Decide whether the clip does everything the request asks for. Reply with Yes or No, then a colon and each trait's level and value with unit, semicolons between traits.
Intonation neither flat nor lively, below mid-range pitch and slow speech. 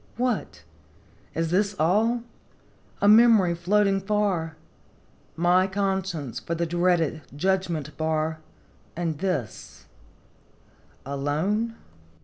No: average, 4.0 semitones; medium, 175 Hz; slow, 90 wpm